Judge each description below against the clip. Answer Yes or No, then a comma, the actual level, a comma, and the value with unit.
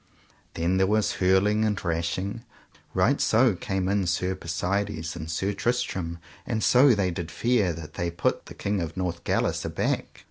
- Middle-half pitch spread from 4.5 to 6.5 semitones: No, average, 3.5 semitones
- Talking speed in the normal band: Yes, average, 165 wpm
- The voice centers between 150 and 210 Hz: No, very low, 95 Hz